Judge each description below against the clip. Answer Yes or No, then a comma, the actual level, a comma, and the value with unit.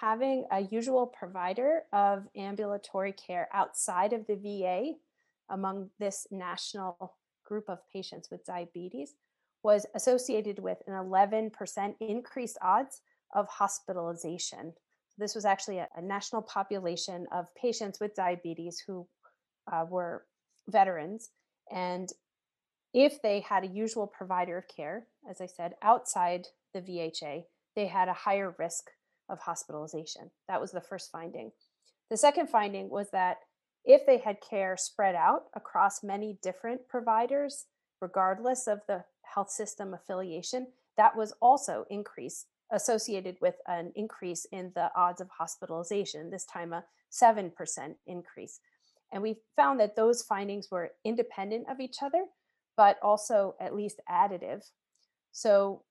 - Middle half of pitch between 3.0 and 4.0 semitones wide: Yes, average, 3.6 semitones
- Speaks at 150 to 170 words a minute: No, slow, 135 wpm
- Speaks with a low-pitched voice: No, high, 200 Hz